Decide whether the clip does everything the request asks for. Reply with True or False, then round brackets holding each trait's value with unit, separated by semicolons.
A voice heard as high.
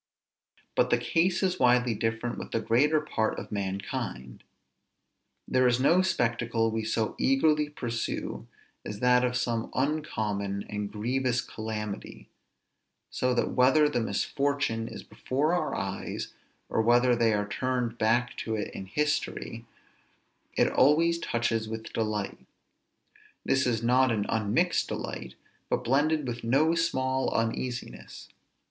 False (120 Hz)